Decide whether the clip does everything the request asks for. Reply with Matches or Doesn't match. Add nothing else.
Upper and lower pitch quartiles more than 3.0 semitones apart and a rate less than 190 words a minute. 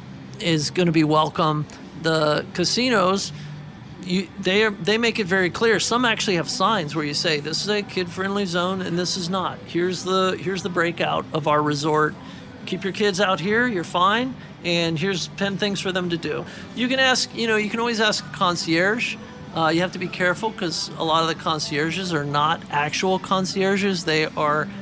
Doesn't match